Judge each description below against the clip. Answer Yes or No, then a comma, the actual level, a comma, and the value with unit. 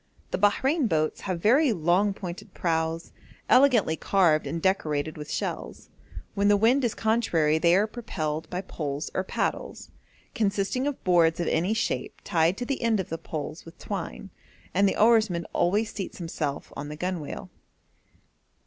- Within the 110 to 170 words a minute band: Yes, average, 160 wpm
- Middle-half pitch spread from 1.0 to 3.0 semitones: No, average, 5.0 semitones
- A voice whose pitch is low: No, medium, 185 Hz